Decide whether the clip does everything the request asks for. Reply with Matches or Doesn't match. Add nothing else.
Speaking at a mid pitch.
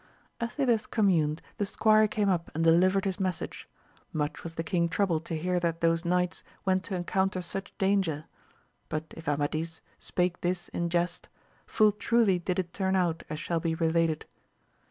Matches